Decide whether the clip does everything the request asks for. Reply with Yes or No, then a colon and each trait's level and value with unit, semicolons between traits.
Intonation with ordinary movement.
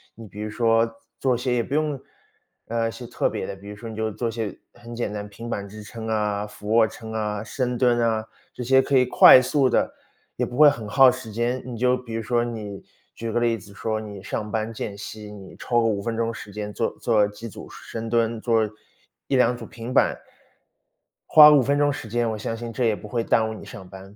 No: narrow, 2.2 semitones